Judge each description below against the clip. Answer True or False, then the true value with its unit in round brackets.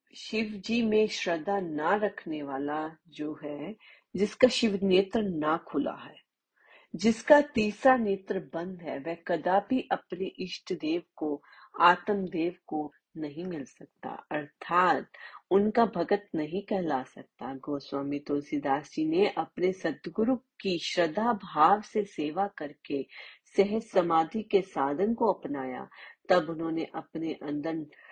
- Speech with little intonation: False (5.4 semitones)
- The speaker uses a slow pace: False (130 wpm)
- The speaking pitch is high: False (180 Hz)